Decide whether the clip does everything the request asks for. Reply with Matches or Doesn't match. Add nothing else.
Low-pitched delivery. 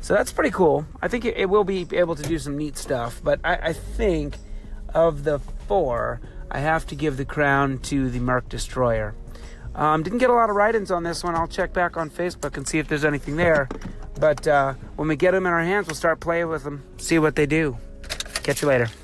Doesn't match